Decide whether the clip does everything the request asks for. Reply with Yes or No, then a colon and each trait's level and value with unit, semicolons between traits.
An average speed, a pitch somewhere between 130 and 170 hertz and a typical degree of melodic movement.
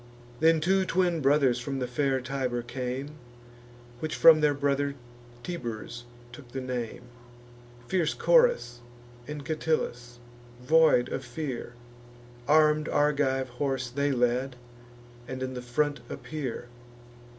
No: slow, 115 wpm; low, 135 Hz; average, 3.6 semitones